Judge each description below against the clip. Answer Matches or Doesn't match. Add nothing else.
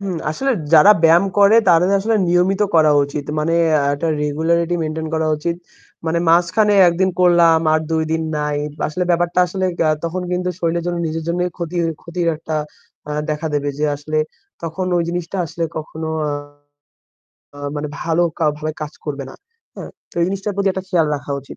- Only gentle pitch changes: Matches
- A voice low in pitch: Doesn't match